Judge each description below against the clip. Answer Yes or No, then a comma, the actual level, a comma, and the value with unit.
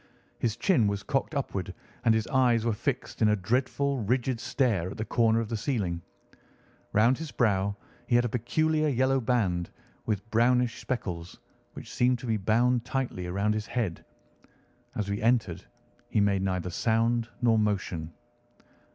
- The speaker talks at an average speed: Yes, average, 160 wpm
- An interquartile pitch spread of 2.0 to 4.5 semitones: Yes, average, 3.7 semitones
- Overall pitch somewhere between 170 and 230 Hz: No, low, 115 Hz